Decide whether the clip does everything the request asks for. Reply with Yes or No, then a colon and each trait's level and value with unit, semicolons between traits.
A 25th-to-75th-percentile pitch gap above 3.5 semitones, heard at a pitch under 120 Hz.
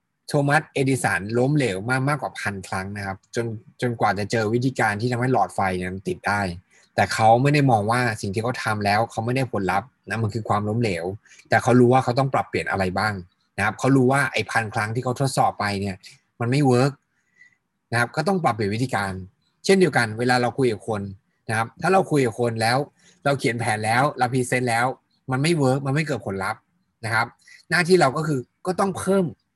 No: average, 4.3 semitones; low, 125 Hz